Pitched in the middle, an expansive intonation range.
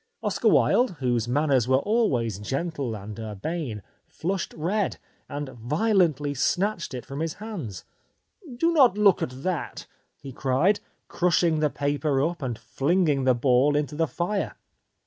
Yes: medium, 150 Hz; wide, 5.8 semitones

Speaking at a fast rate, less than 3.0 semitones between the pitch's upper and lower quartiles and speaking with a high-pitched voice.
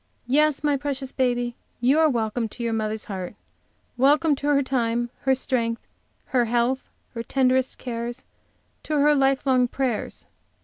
No: average, 150 wpm; narrow, 2.6 semitones; very high, 255 Hz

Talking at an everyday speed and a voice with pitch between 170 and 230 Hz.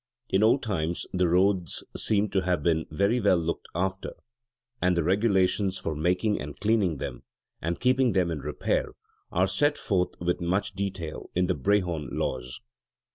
No: average, 165 wpm; very low, 90 Hz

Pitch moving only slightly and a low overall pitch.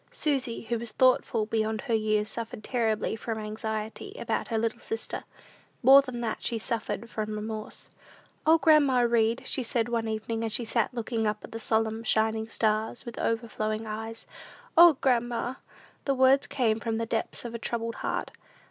No: narrow, 1.8 semitones; high, 225 Hz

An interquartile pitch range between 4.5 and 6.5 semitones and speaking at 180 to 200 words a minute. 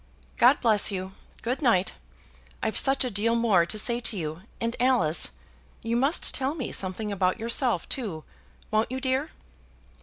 No: average, 4.9 semitones; average, 160 wpm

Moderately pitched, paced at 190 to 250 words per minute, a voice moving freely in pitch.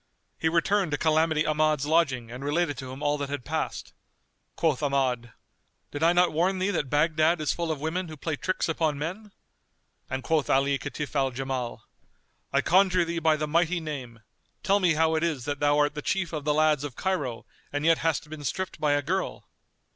No: medium, 155 Hz; fast, 205 wpm; average, 2.9 semitones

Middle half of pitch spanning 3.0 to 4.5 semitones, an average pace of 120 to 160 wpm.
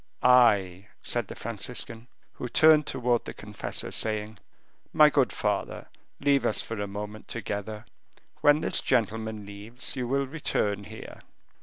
Yes: average, 3.4 semitones; average, 140 wpm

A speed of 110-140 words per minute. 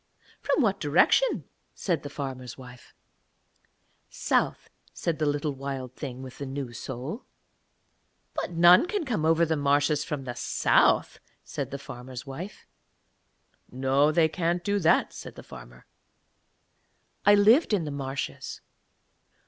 Yes: slow, 135 wpm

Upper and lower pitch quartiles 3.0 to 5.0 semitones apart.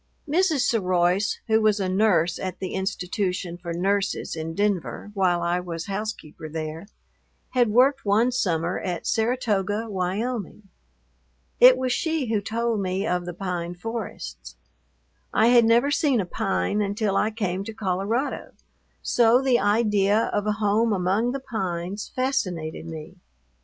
Yes: average, 4.1 semitones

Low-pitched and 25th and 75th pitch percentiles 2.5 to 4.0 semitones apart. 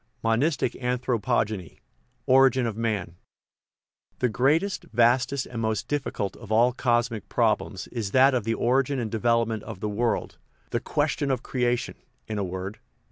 Yes: low, 120 Hz; average, 2.8 semitones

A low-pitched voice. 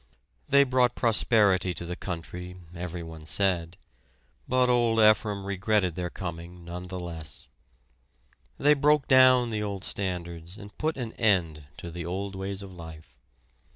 Yes: very low, 95 Hz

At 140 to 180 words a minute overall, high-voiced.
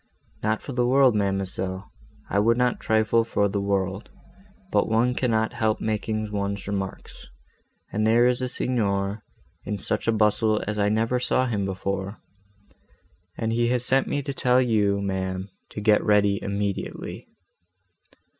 No: average, 155 wpm; low, 105 Hz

